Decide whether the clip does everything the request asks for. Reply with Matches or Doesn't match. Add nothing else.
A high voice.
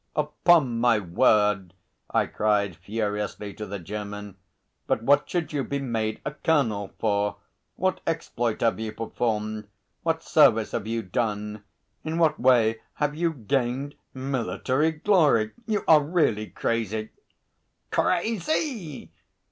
Doesn't match